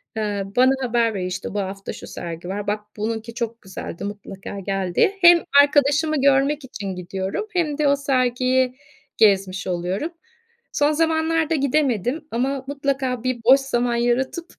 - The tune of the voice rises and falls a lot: Yes, wide, 5.8 semitones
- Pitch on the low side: No, high, 245 Hz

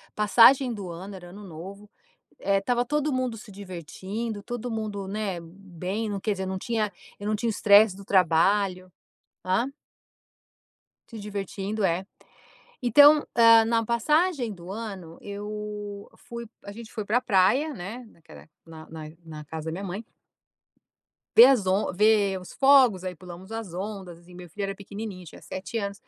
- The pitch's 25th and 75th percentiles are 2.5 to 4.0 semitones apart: Yes, average, 3.4 semitones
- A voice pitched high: Yes, high, 205 Hz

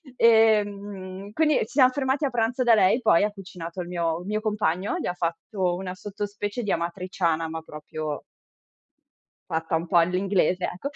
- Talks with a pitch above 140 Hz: Yes, high, 190 Hz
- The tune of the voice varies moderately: Yes, average, 3.9 semitones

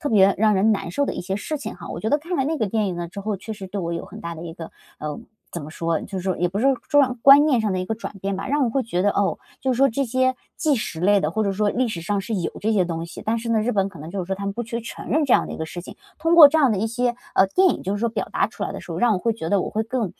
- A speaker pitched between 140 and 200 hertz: No, high, 210 Hz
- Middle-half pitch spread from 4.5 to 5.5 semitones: Yes, average, 4.8 semitones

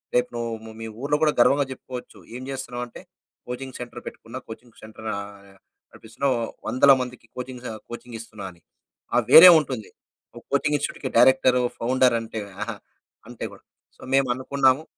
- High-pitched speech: No, low, 125 Hz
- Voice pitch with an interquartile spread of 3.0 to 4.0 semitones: No, narrow, 2.6 semitones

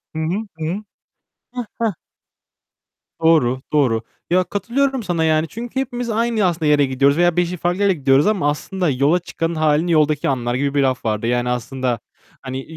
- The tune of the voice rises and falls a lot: Yes, wide, 5.9 semitones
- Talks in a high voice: No, medium, 155 Hz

